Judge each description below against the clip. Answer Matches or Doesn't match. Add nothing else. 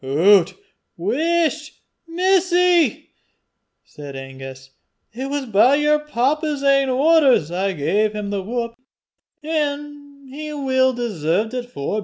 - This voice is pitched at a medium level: Doesn't match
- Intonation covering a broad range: Matches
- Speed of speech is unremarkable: Doesn't match